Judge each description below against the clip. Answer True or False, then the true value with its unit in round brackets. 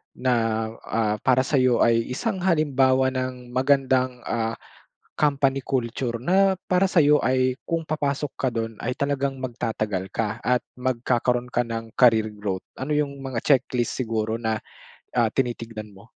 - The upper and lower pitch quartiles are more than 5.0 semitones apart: False (3.1 semitones)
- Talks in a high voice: False (125 Hz)